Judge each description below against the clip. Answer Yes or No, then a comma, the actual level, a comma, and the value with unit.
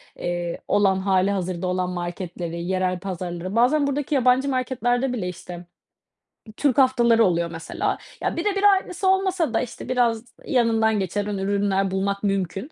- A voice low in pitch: No, high, 200 Hz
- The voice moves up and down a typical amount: No, wide, 5.7 semitones